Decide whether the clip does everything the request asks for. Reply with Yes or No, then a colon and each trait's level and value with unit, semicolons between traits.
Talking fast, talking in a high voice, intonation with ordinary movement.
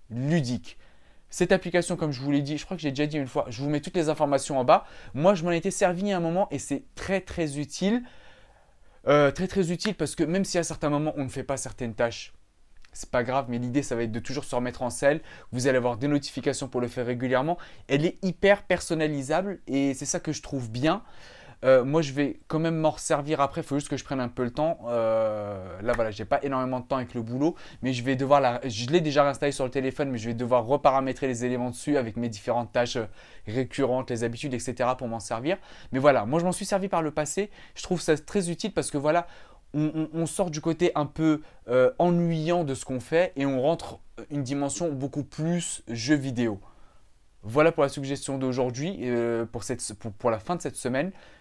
No: fast, 240 wpm; medium, 140 Hz; average, 4.5 semitones